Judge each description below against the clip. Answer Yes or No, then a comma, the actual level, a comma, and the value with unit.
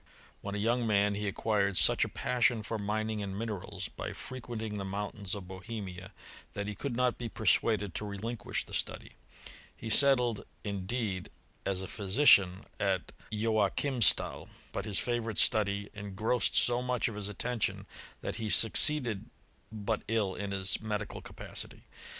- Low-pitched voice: Yes, low, 105 Hz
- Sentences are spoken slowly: No, average, 155 wpm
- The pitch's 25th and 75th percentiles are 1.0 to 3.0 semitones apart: Yes, narrow, 2.5 semitones